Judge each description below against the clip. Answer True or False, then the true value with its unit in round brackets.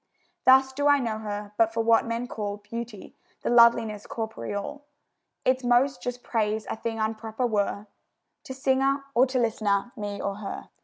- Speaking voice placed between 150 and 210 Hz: False (230 Hz)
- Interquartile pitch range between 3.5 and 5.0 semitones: False (3.0 semitones)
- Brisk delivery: False (165 wpm)